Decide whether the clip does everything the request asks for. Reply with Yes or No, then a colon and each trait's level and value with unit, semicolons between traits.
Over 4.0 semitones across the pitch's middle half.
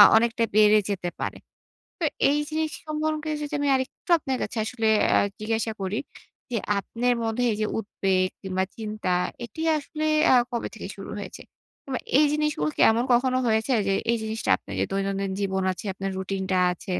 Yes: average, 5.0 semitones